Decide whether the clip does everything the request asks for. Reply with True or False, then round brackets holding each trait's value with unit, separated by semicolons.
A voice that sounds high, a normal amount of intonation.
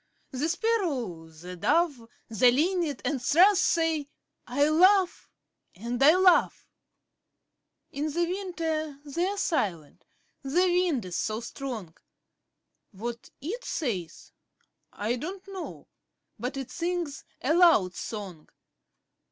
False (290 Hz; 7.1 semitones)